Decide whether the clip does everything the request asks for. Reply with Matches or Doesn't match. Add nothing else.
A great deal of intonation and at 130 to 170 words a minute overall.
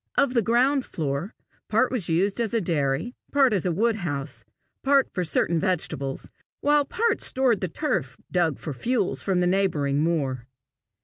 Matches